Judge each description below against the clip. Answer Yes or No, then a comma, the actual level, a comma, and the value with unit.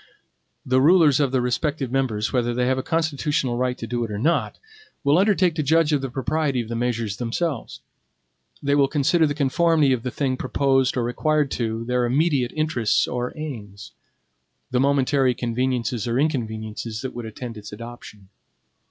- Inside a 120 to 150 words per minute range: No, average, 175 wpm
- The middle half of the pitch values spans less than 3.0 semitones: No, average, 3.7 semitones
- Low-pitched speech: Yes, low, 130 Hz